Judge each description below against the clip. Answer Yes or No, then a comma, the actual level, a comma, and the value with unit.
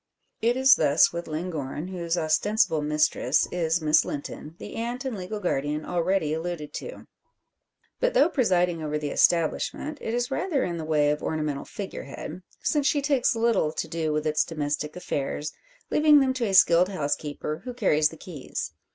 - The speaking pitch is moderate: Yes, medium, 170 Hz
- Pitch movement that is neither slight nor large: No, wide, 6.9 semitones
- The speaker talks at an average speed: Yes, average, 175 wpm